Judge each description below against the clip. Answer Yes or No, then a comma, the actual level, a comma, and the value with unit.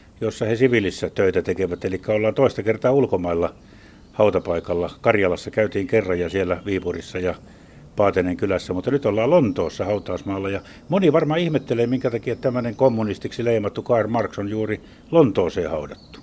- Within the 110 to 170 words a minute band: Yes, average, 150 wpm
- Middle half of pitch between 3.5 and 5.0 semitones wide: Yes, average, 4.5 semitones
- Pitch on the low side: Yes, low, 105 Hz